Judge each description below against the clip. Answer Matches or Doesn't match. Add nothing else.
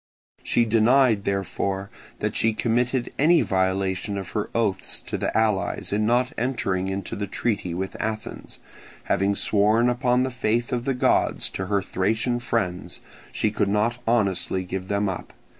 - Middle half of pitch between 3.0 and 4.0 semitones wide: Matches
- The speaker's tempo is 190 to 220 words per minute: Doesn't match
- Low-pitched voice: Matches